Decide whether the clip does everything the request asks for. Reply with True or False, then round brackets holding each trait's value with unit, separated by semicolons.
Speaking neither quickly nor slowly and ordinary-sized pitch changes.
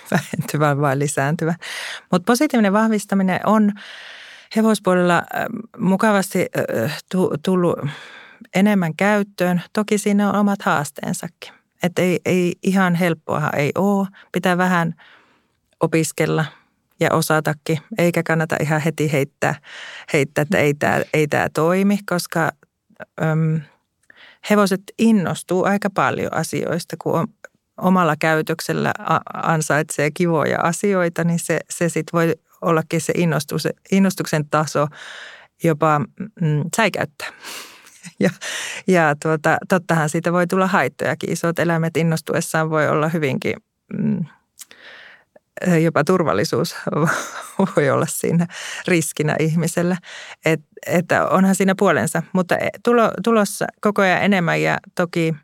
True (110 wpm; 3.5 semitones)